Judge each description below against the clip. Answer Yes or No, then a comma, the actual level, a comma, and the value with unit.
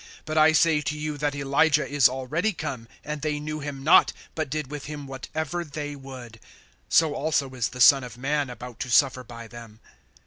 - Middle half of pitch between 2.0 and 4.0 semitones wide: Yes, average, 2.9 semitones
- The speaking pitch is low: No, medium, 145 Hz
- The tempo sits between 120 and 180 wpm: No, average, 200 wpm